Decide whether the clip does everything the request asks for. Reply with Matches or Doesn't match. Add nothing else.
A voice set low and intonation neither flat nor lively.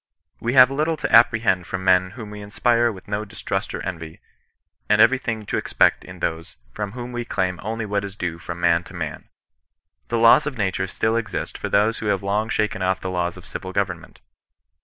Matches